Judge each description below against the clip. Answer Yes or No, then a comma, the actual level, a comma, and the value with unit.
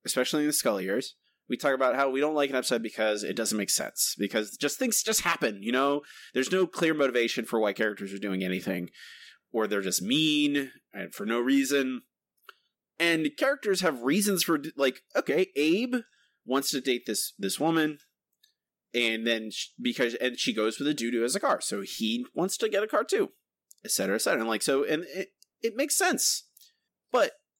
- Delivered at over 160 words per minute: Yes, average, 200 wpm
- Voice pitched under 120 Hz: No, medium, 140 Hz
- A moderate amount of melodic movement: No, wide, 8.7 semitones